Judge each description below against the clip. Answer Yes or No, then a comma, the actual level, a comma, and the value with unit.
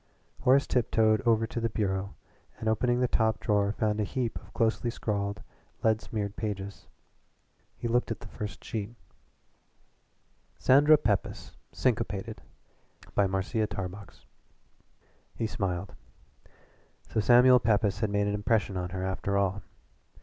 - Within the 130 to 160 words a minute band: Yes, slow, 135 wpm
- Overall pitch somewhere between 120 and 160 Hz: No, low, 105 Hz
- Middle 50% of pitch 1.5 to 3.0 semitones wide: Yes, narrow, 2.4 semitones